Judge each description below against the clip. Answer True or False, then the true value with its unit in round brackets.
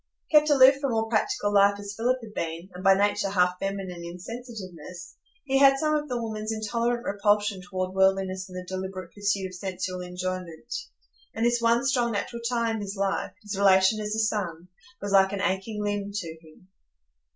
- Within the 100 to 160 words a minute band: False (185 wpm)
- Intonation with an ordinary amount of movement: True (3.4 semitones)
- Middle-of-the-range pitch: False (200 Hz)